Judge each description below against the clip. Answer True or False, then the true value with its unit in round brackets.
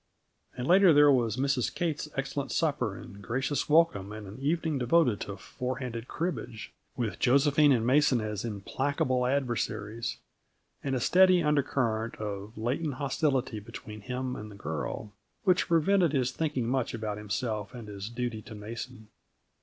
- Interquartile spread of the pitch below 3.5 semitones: False (4.8 semitones)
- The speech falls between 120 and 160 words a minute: True (155 wpm)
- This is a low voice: True (125 Hz)